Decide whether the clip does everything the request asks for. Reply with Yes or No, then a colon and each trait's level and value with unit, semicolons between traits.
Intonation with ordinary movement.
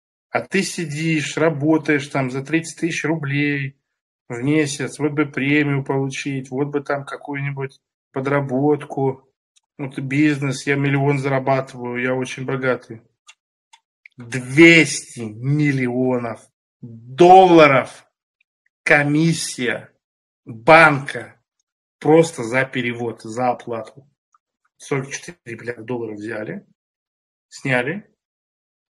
Yes: average, 3.0 semitones